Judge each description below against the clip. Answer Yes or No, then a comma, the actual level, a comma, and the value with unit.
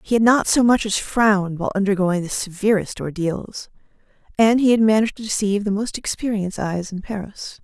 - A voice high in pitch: Yes, high, 205 Hz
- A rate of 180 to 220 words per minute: Yes, average, 190 wpm